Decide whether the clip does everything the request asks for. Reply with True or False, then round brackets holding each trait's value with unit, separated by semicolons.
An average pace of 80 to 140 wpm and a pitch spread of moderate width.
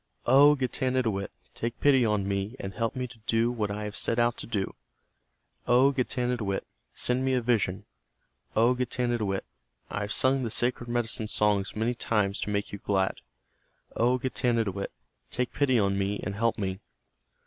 False (165 wpm; 3.4 semitones)